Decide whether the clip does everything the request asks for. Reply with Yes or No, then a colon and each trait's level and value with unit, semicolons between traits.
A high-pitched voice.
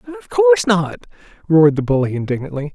No: medium, 145 Hz